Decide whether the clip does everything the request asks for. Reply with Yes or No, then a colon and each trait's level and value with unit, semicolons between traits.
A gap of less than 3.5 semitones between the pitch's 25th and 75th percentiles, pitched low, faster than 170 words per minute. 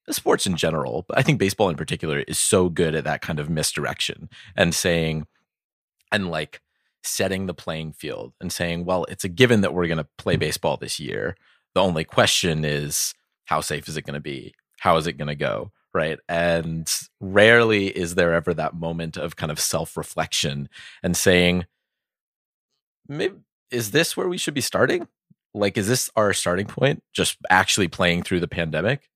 No: average, 3.8 semitones; very low, 90 Hz; average, 185 wpm